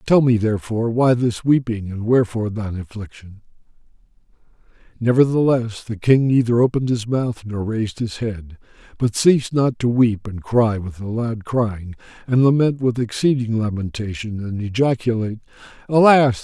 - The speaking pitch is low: Yes, low, 115 Hz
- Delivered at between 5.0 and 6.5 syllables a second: Yes, 5.2 syllables/s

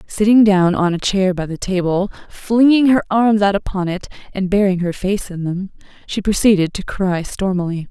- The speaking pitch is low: No, high, 195 Hz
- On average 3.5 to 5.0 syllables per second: Yes, 4.9 syllables/s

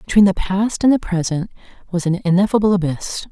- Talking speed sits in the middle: Yes, average, 180 wpm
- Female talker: Yes, female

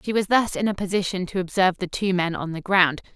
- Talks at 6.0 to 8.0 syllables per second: Yes, 6.1 syllables/s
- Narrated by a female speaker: Yes, female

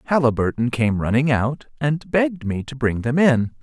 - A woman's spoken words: No, male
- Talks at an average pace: Yes, average, 180 wpm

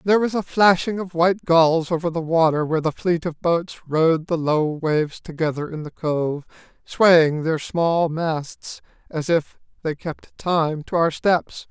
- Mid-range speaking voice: Yes, medium, 165 Hz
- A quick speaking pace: No, average, 180 wpm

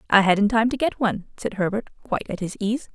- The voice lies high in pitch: Yes, high, 215 Hz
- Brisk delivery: Yes, fast, 245 wpm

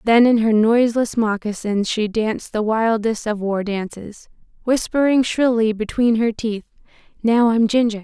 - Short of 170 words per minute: Yes, average, 150 wpm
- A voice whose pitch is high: Yes, high, 225 Hz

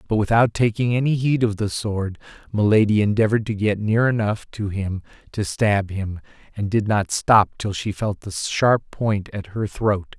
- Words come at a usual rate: Yes, average, 190 wpm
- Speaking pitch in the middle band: No, low, 105 Hz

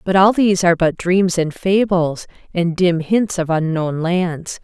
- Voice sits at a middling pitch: Yes, medium, 175 Hz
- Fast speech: No, average, 180 wpm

